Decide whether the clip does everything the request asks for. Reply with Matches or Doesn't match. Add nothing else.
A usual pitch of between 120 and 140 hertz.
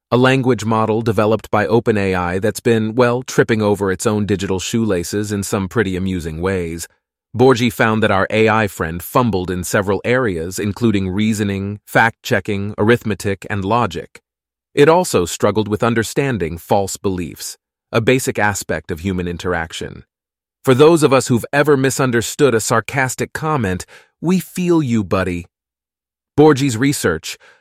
Doesn't match